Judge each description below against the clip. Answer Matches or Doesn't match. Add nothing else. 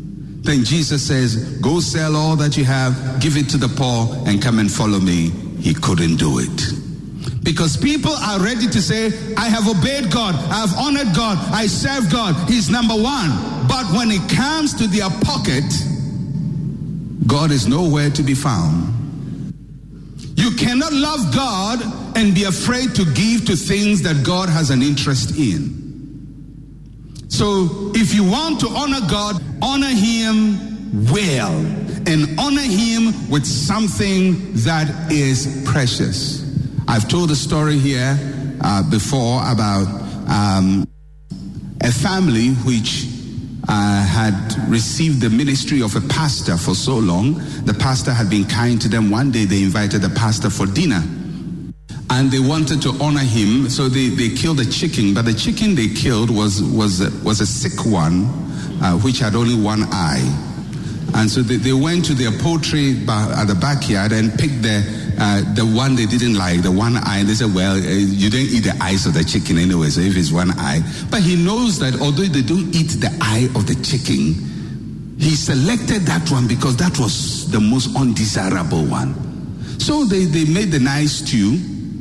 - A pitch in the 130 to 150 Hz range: Matches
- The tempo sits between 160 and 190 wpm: Matches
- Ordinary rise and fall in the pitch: Doesn't match